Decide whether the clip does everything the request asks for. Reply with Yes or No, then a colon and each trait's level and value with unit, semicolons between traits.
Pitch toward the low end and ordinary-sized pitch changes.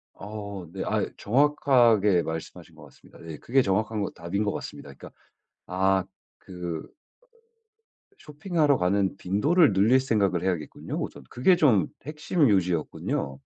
No: low, 100 Hz; wide, 6.4 semitones